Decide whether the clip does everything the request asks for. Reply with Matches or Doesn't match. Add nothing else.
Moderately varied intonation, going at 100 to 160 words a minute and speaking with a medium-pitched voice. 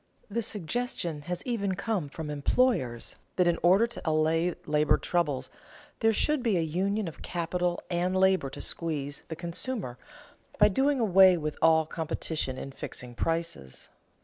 Matches